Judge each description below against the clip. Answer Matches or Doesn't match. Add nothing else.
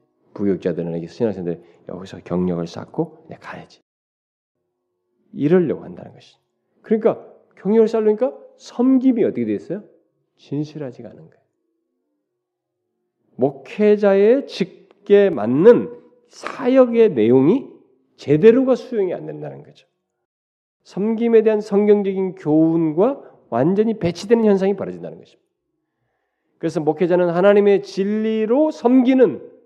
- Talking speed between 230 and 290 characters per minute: Matches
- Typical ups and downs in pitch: Doesn't match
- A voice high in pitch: Matches